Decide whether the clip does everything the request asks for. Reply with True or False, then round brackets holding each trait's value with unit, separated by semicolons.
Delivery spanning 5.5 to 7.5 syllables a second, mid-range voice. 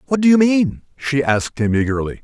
True (5.9 syllables/s; 145 Hz)